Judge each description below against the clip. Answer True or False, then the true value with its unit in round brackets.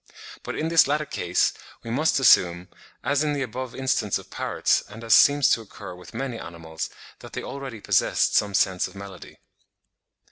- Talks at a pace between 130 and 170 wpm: False (180 wpm)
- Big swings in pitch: True (6.8 semitones)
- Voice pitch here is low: True (115 Hz)